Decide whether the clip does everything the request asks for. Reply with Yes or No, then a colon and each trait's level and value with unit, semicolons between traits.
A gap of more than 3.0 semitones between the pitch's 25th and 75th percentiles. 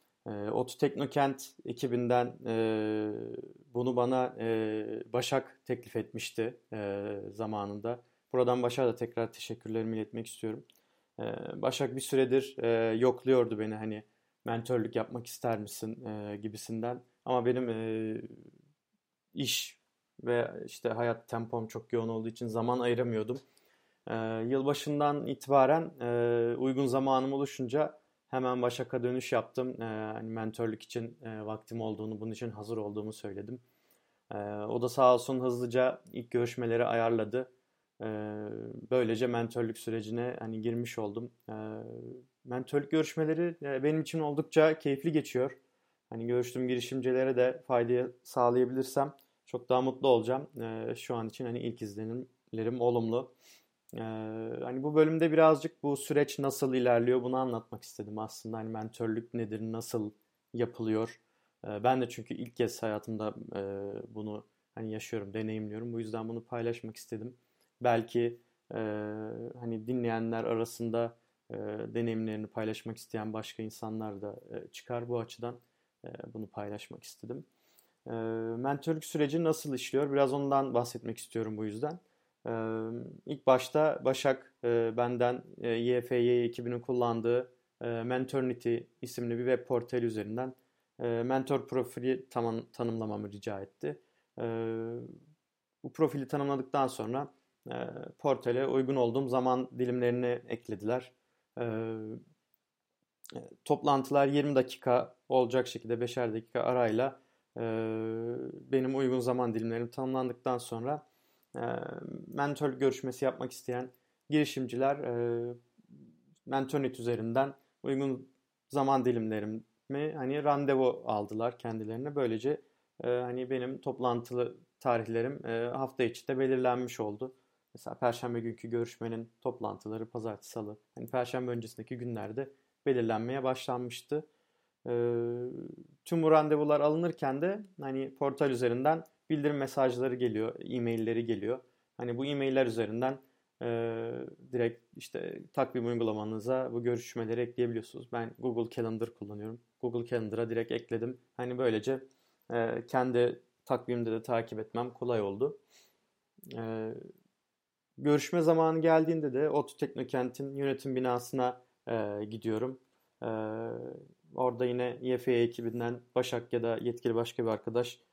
No: narrow, 2.4 semitones